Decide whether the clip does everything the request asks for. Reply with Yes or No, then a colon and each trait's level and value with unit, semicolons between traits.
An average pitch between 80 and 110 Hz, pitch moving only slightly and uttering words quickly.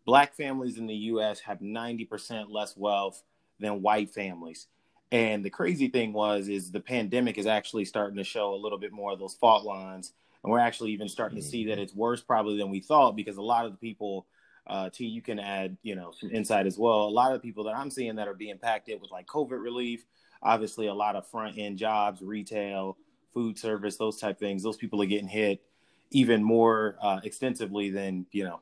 Yes: low, 105 Hz; narrow, 2.2 semitones; fast, 225 wpm